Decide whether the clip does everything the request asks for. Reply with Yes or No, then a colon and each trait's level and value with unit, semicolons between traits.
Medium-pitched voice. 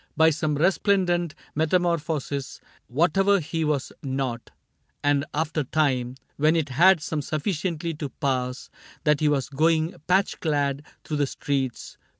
Yes: medium, 150 Hz